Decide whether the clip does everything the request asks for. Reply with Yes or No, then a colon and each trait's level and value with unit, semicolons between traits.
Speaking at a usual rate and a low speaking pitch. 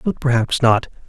Yes: average, 165 wpm; low, 130 Hz